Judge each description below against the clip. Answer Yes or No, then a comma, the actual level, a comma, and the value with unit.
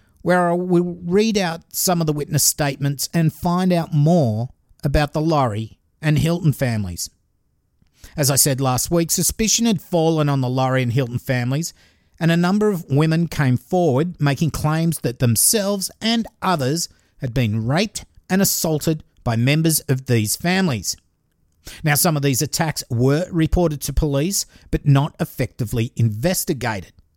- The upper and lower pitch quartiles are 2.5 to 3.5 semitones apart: No, average, 5.3 semitones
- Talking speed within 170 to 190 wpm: No, average, 155 wpm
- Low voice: No, medium, 150 Hz